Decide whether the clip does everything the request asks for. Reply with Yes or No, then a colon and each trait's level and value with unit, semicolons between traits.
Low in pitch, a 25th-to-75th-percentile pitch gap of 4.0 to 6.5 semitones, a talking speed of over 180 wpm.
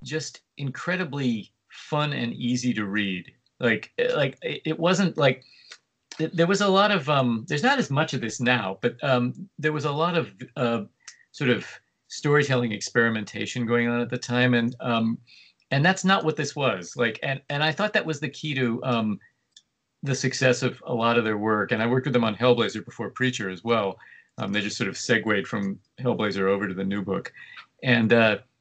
Yes: low, 125 Hz; average, 4.7 semitones; average, 200 wpm